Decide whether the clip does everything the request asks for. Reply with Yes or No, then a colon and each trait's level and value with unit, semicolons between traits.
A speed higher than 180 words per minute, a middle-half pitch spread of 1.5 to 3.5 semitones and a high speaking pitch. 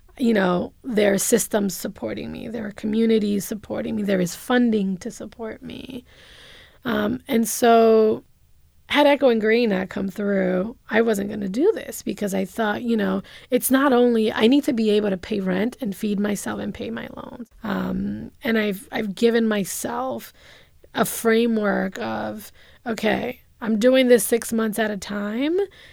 No: average, 175 wpm; average, 2.9 semitones; high, 220 Hz